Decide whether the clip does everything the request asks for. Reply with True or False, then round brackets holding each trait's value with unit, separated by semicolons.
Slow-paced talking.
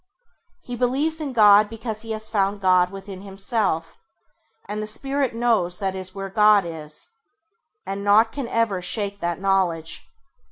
False (155 wpm)